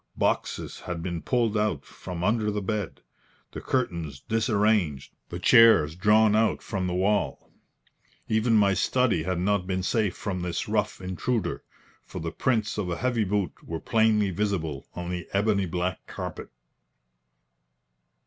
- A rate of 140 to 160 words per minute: Yes, average, 150 wpm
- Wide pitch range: No, average, 3.6 semitones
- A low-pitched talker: Yes, low, 100 Hz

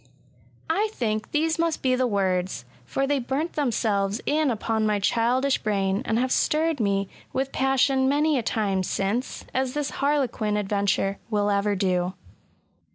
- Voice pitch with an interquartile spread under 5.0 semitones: No, average, 5.3 semitones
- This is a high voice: Yes, high, 230 Hz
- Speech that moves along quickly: No, average, 155 wpm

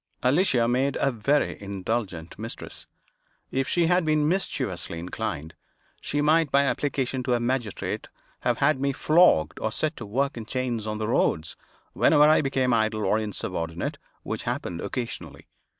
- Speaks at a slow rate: No, average, 155 wpm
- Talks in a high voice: No, low, 125 Hz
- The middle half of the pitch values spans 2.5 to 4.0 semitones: No, average, 5.1 semitones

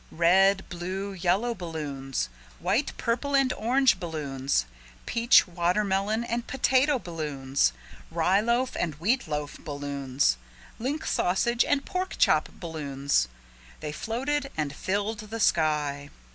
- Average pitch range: No, wide, 7.7 semitones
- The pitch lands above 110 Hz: Yes, medium, 185 Hz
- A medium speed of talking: No, slow, 115 wpm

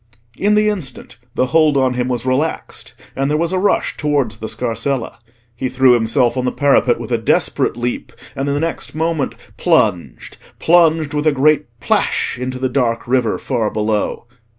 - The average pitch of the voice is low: Yes, low, 130 Hz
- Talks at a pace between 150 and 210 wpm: Yes, average, 175 wpm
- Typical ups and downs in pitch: Yes, average, 4.1 semitones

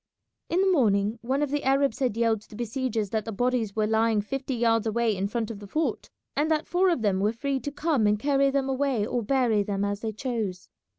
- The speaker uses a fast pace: Yes, fast, 240 wpm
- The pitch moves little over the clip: No, average, 4.4 semitones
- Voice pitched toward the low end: No, high, 230 Hz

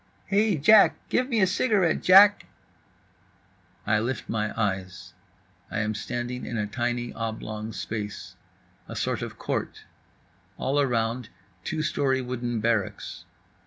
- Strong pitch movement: Yes, wide, 5.9 semitones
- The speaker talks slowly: Yes, slow, 125 wpm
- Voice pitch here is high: No, low, 120 Hz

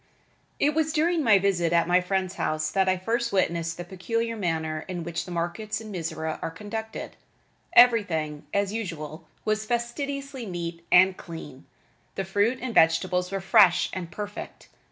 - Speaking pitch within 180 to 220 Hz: Yes, high, 190 Hz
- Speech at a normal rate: Yes, average, 160 wpm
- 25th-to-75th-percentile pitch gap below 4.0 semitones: No, average, 4.7 semitones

